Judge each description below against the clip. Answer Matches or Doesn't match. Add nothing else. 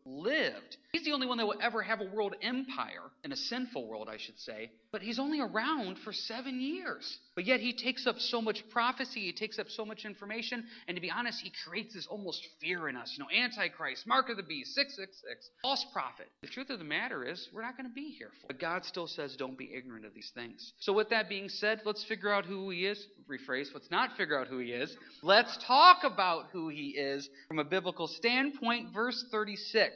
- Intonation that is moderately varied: Doesn't match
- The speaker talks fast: Matches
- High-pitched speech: Matches